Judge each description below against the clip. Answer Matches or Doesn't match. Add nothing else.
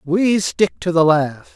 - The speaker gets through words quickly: Doesn't match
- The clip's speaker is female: Doesn't match